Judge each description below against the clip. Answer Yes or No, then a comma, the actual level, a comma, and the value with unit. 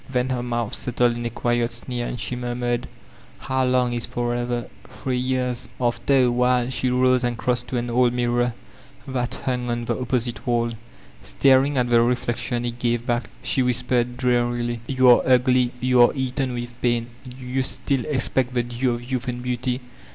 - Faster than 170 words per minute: Yes, average, 190 wpm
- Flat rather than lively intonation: Yes, narrow, 1.0 semitones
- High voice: No, low, 125 Hz